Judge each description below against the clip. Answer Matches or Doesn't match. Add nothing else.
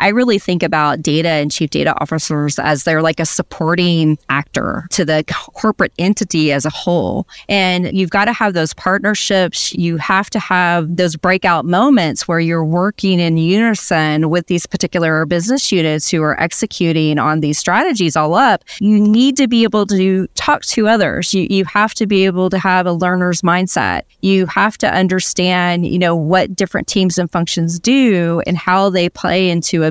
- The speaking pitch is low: Doesn't match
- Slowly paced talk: Doesn't match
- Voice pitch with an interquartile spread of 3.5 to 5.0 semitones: Doesn't match